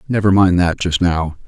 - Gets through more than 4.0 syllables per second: Yes, 4.8 syllables/s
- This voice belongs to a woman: No, male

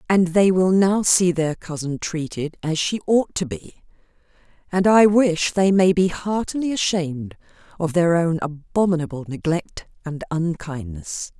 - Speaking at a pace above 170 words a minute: No, average, 145 wpm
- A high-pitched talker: No, medium, 170 Hz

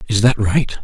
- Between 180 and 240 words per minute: Yes, fast, 215 wpm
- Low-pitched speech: Yes, low, 115 Hz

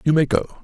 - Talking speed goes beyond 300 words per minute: No, fast, 285 wpm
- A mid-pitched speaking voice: Yes, medium, 150 Hz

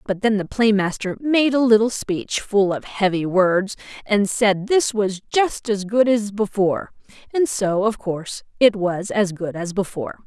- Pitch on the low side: No, high, 205 Hz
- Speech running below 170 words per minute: No, average, 180 wpm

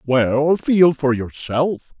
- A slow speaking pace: Yes, slow, 120 wpm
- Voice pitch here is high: No, medium, 140 Hz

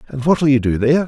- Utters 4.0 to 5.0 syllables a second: No, 6.6 syllables/s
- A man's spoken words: Yes, male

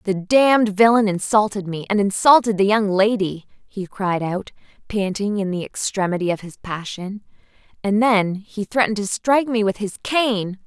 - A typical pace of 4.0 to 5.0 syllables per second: Yes, 4.7 syllables/s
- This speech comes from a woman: Yes, female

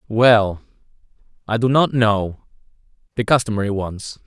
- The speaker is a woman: No, male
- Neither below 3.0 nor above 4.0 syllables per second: No, 4.4 syllables/s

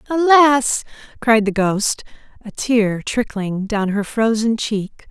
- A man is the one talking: No, female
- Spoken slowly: Yes, slow, 130 wpm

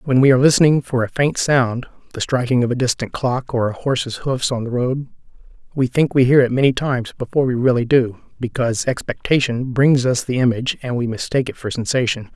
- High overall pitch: No, low, 125 Hz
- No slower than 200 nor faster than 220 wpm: Yes, fast, 205 wpm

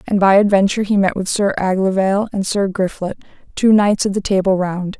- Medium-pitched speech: No, high, 195 Hz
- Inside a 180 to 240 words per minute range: Yes, fast, 205 wpm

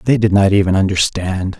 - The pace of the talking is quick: No, average, 190 wpm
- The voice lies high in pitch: No, low, 100 Hz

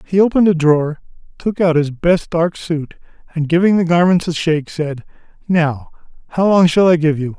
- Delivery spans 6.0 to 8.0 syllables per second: No, 5.3 syllables/s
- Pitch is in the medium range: Yes, medium, 165 Hz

